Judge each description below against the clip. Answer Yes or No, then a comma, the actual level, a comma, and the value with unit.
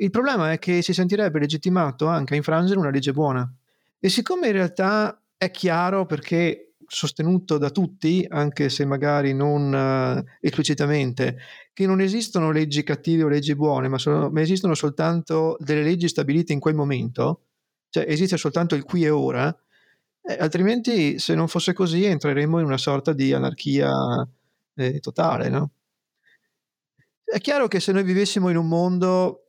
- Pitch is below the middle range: No, medium, 160 Hz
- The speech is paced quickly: No, average, 160 wpm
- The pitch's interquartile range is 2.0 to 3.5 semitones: No, average, 4.0 semitones